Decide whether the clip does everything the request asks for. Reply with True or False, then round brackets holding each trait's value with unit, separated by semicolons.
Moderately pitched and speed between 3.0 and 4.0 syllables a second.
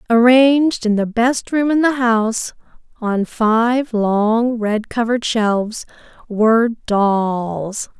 False (225 Hz; 3.4 syllables/s)